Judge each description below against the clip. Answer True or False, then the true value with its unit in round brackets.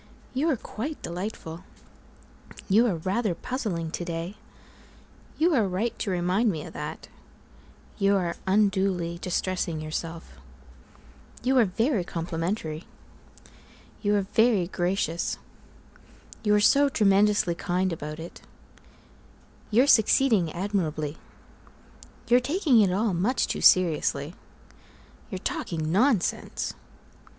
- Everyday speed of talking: False (110 wpm)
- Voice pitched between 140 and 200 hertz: True (190 Hz)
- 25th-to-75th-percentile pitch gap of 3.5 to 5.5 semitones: True (4.6 semitones)